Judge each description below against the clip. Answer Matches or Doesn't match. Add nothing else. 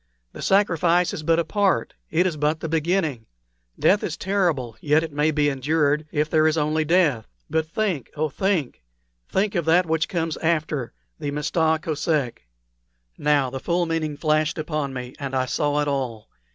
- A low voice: Doesn't match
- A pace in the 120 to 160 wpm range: Doesn't match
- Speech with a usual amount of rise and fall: Doesn't match